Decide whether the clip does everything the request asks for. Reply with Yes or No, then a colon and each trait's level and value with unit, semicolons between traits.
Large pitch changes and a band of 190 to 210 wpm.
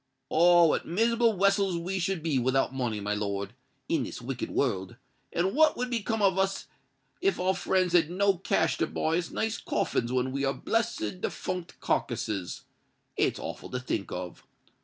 No: wide, 7.5 semitones; average, 165 wpm